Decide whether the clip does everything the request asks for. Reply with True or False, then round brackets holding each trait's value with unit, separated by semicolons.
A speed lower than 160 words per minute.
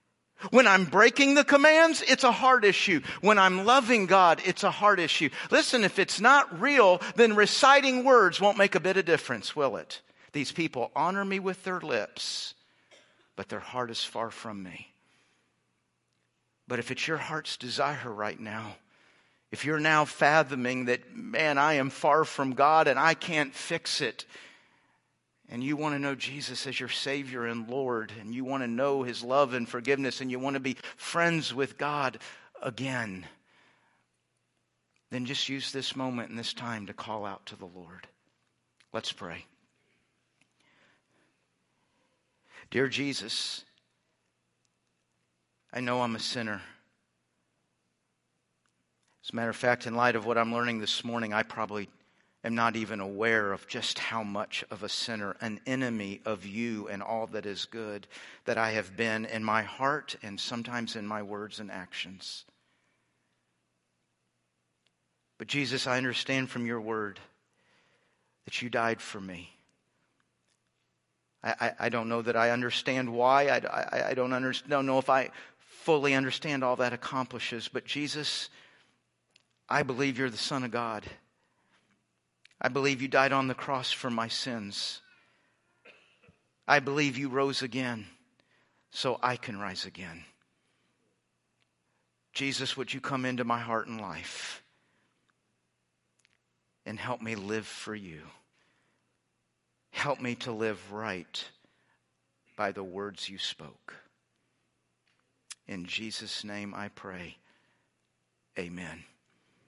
True (145 wpm)